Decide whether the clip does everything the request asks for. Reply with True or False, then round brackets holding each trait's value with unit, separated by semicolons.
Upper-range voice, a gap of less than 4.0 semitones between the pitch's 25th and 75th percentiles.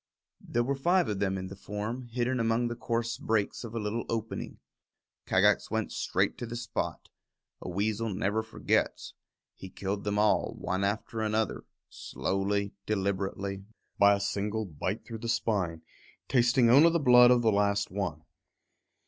False (110 Hz; 2.9 semitones)